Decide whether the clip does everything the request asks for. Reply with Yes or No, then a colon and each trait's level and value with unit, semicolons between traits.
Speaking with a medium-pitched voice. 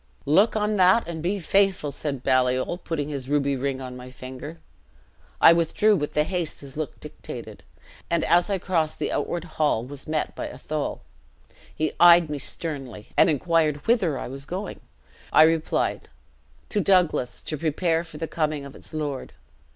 Yes: medium, 155 Hz